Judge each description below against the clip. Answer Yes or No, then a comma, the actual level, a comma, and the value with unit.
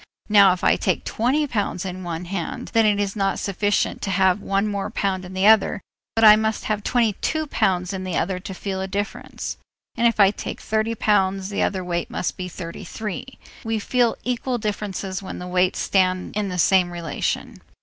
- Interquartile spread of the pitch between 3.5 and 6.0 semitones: No, average, 2.7 semitones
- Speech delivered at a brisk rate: Yes, fast, 210 wpm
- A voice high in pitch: Yes, high, 195 Hz